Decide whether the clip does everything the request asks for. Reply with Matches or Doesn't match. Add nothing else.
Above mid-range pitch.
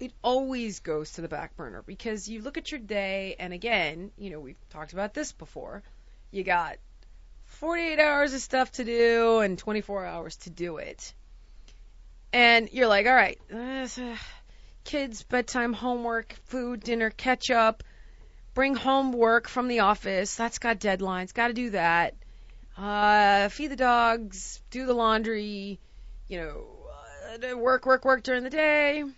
Matches